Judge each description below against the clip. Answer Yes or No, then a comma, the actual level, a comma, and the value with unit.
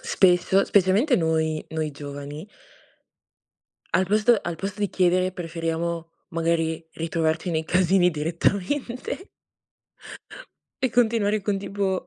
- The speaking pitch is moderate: Yes, medium, 180 Hz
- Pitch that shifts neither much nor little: Yes, average, 3.7 semitones